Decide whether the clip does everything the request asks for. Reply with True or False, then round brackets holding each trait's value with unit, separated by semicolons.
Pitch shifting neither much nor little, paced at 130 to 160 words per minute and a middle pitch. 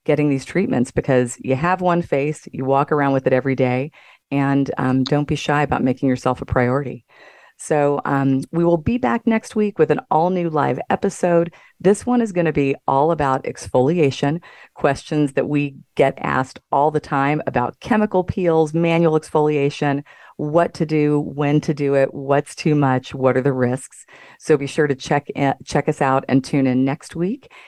False (3.4 semitones; 195 wpm; 145 Hz)